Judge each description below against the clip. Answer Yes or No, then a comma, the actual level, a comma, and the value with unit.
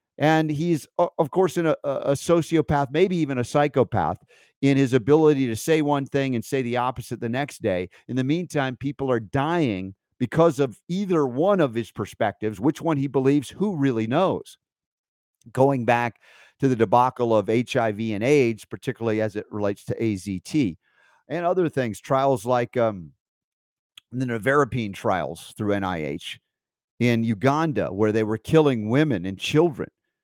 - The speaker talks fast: No, average, 160 wpm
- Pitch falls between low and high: No, low, 130 Hz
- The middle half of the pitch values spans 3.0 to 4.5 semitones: No, average, 4.9 semitones